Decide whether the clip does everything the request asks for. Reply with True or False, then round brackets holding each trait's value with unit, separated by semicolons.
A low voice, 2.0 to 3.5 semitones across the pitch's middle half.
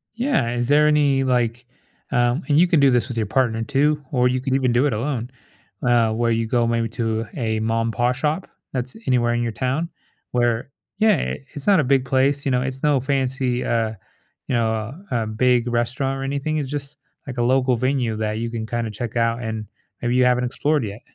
True (125 Hz; 2.8 semitones)